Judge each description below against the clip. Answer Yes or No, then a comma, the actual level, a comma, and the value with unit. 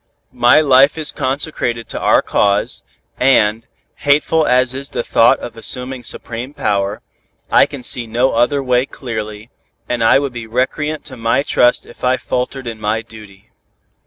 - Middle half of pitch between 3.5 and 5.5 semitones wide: No, average, 3.0 semitones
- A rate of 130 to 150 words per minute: No, average, 160 wpm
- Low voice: Yes, low, 125 Hz